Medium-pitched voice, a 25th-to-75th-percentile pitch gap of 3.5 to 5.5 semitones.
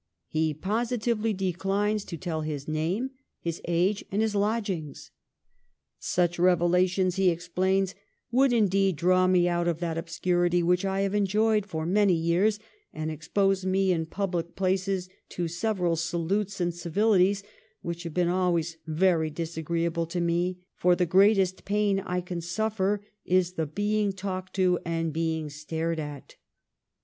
No: medium, 180 Hz; average, 2.7 semitones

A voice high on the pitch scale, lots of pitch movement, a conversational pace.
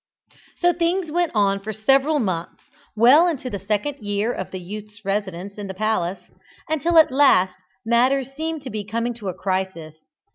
Yes: high, 220 Hz; wide, 6.5 semitones; average, 160 wpm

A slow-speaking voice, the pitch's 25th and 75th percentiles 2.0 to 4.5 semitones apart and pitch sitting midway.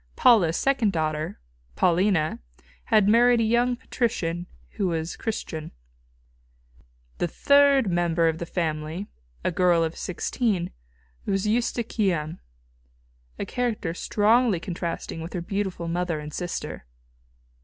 No: slow, 115 wpm; average, 5.1 semitones; medium, 180 Hz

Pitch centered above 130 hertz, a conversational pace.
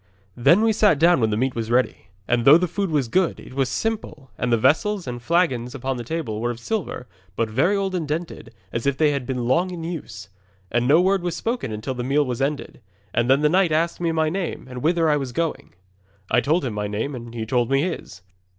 No: medium, 140 Hz; fast, 240 wpm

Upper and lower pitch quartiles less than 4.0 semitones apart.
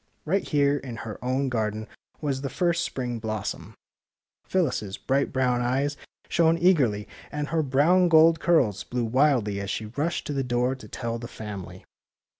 No: average, 5.1 semitones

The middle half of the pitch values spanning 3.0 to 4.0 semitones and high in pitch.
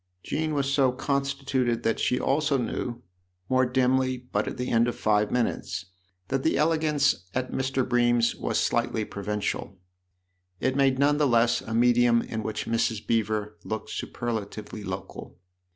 No: average, 3.3 semitones; low, 125 Hz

